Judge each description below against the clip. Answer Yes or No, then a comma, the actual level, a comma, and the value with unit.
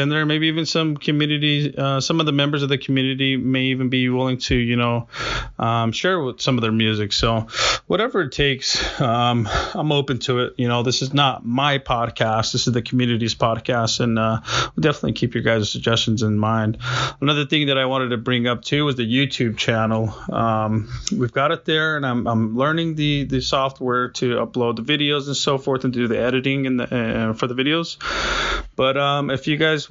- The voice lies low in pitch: Yes, low, 130 Hz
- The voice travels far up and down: No, average, 3.2 semitones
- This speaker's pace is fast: Yes, fast, 215 wpm